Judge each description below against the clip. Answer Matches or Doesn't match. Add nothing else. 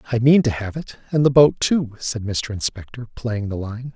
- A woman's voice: Doesn't match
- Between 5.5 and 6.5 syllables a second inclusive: Doesn't match